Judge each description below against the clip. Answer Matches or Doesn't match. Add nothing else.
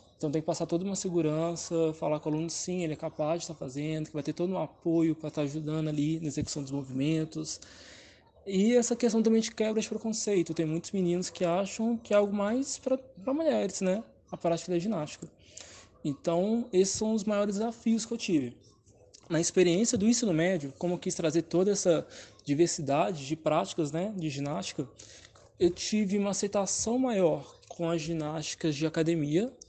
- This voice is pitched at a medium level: Matches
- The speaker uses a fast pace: Matches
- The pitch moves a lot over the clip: Doesn't match